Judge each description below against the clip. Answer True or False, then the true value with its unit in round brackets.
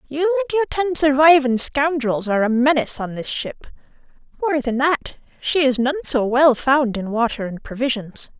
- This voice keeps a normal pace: True (180 wpm)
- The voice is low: False (270 Hz)